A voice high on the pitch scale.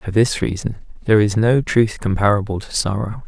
No: low, 105 Hz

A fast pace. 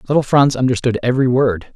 No: average, 170 wpm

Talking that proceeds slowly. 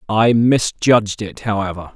Yes: slow, 125 wpm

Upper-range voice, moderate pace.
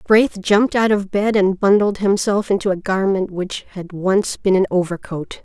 Yes: high, 195 Hz; average, 190 wpm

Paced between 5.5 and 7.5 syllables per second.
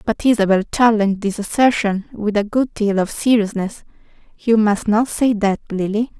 No: 4.9 syllables/s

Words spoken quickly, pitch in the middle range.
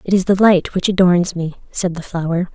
Yes: fast, 235 wpm; medium, 180 Hz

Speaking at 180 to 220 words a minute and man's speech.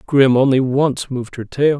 Yes: average, 200 wpm; male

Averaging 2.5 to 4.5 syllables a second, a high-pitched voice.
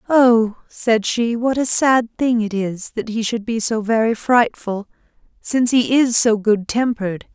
Yes: 4.1 syllables/s; high, 230 Hz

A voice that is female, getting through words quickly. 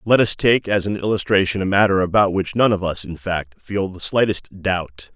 No: male; fast, 220 wpm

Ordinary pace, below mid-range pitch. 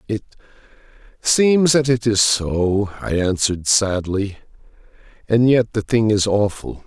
No: slow, 130 wpm; low, 110 Hz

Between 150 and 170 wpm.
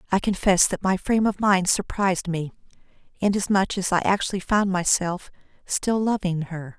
Yes: average, 160 wpm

